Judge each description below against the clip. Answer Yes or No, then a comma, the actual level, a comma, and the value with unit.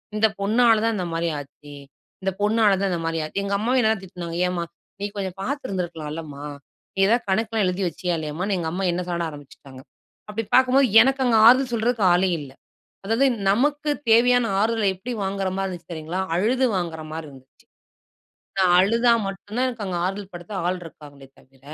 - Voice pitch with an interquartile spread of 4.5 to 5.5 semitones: Yes, average, 5.1 semitones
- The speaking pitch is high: Yes, high, 195 Hz